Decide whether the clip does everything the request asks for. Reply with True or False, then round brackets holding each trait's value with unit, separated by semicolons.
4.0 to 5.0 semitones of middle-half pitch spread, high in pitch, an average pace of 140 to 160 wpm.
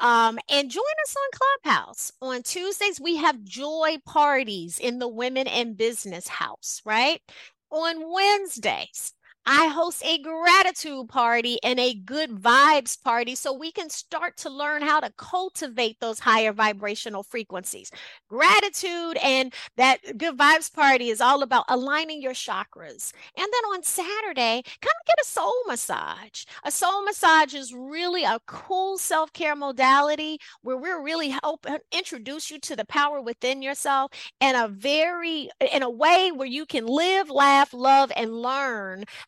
True (4.6 semitones; 285 Hz; 150 wpm)